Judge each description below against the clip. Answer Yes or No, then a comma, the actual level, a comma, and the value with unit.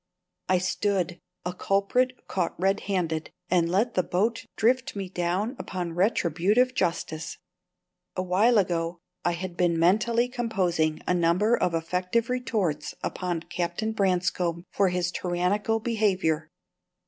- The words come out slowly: Yes, slow, 130 wpm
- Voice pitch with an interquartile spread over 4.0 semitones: No, average, 3.7 semitones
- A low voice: No, medium, 185 Hz